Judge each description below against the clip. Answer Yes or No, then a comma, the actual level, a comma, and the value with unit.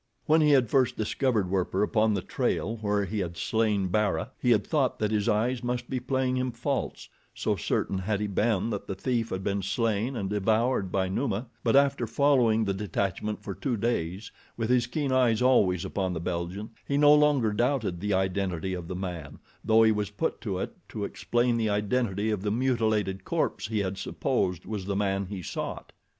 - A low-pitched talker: Yes, low, 105 Hz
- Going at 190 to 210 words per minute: Yes, average, 200 wpm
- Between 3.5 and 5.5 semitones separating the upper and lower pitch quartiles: Yes, average, 3.9 semitones